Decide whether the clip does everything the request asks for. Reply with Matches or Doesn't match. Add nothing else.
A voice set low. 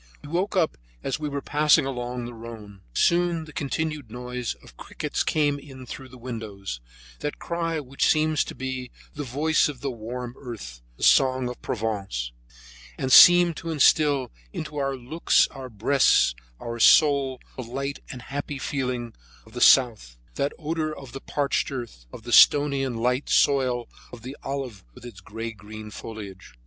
Matches